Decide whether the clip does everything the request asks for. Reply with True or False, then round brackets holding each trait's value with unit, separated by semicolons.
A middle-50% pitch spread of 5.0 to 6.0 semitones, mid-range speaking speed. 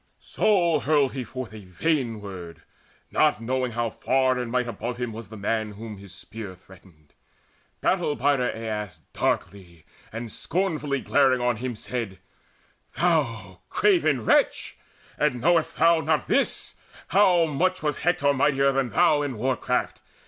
True (5.6 semitones; 150 wpm)